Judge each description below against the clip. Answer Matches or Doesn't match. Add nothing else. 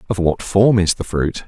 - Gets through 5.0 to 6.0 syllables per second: Doesn't match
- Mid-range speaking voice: Doesn't match